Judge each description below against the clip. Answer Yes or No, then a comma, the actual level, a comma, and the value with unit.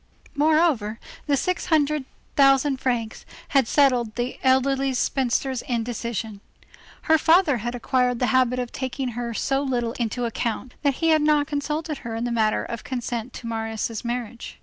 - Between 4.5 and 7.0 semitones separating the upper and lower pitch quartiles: No, average, 3.1 semitones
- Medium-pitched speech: No, very high, 250 Hz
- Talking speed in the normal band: Yes, average, 160 wpm